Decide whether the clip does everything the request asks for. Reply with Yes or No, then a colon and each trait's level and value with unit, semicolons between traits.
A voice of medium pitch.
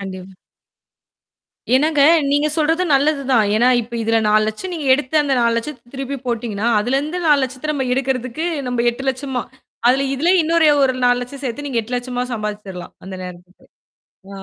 No: very high, 255 Hz